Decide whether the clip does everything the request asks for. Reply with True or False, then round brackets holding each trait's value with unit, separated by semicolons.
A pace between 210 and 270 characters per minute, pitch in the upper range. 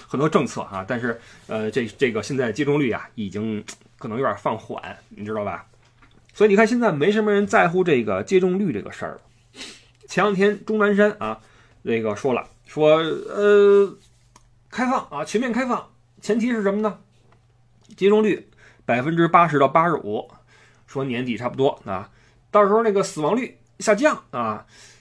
False (260 characters per minute; 155 Hz)